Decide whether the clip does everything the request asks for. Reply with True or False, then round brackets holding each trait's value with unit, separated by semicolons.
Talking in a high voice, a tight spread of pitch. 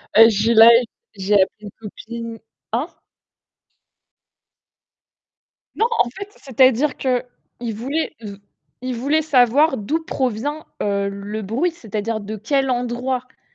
False (240 Hz; 3.8 semitones)